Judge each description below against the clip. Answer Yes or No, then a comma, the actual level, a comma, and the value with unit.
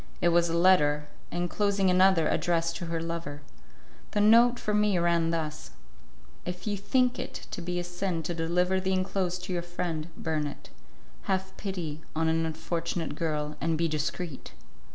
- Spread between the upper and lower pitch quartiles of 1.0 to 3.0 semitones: Yes, narrow, 2.4 semitones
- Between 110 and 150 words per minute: No, average, 170 wpm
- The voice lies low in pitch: No, medium, 175 Hz